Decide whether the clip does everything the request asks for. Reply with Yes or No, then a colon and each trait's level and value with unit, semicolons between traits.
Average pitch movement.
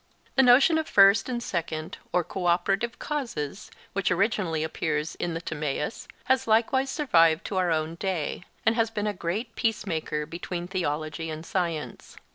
No: wide, 5.8 semitones